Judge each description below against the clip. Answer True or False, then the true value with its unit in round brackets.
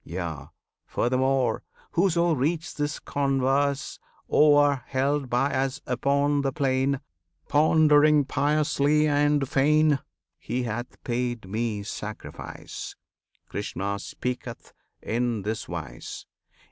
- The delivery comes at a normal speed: False (95 wpm)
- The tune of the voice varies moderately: True (3.4 semitones)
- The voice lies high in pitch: False (135 Hz)